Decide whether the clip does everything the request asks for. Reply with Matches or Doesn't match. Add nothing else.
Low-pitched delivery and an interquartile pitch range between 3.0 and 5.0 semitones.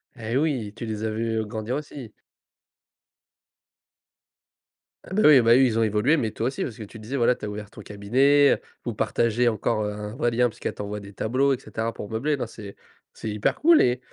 Matches